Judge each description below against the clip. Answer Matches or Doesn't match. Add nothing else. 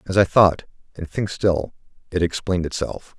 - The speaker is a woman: Doesn't match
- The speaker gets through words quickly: Doesn't match